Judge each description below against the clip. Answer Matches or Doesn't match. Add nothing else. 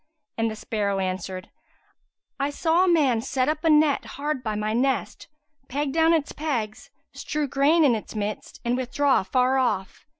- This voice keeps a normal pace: Matches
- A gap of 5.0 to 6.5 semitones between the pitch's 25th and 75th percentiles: Matches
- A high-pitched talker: Matches